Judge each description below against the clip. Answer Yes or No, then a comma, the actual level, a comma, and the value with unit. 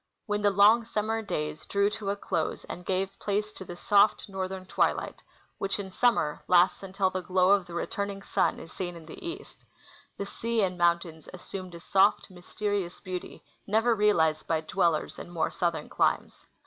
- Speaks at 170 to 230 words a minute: Yes, average, 185 wpm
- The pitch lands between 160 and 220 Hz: Yes, high, 190 Hz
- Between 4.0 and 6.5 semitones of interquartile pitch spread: No, average, 2.8 semitones